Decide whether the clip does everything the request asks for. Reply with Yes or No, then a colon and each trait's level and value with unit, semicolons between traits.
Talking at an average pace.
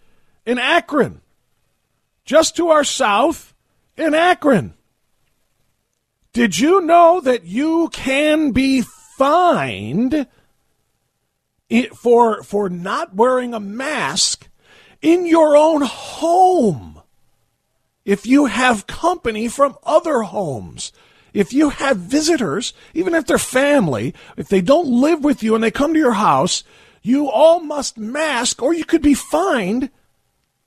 No: slow, 120 wpm